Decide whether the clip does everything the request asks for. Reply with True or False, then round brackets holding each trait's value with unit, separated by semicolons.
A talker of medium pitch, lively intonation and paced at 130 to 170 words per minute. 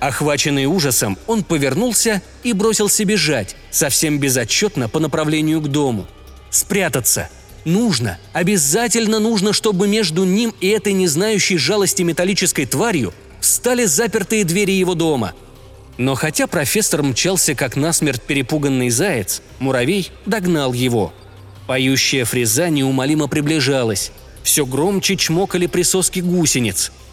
False (160 Hz; 6.7 semitones; 115 wpm)